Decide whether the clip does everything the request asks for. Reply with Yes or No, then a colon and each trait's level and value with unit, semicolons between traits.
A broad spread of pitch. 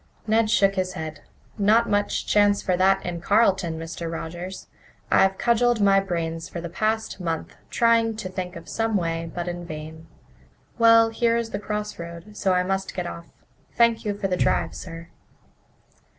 No: average, 4.1 semitones